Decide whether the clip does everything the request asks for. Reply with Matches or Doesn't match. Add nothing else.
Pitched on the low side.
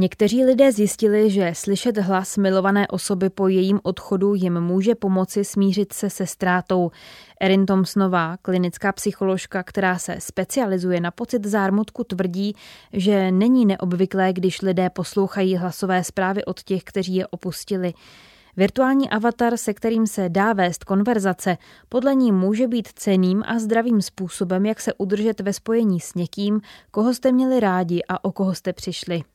Doesn't match